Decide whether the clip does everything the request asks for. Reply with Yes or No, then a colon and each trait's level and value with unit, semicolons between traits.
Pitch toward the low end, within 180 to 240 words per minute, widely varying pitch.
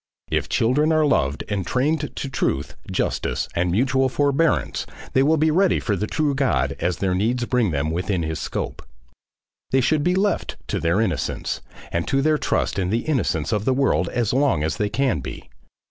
Yes: low, 125 Hz; average, 190 wpm; wide, 7.9 semitones